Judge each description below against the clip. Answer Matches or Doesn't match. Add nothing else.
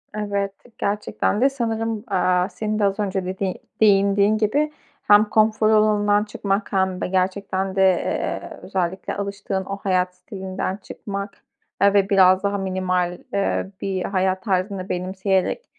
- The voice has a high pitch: Matches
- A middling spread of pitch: Doesn't match